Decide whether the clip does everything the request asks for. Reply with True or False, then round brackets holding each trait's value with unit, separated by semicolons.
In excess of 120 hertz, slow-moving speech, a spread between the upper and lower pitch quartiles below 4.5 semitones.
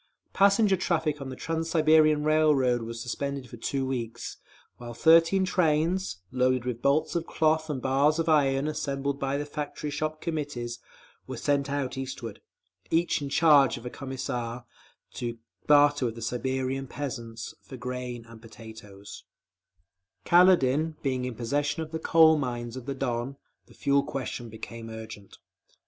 False (135 Hz; 155 wpm; 4.1 semitones)